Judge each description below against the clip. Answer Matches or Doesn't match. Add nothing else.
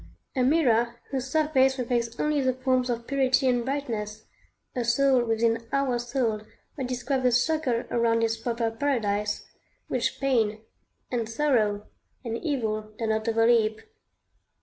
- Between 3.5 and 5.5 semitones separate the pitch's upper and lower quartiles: Doesn't match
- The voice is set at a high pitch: Matches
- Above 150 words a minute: Doesn't match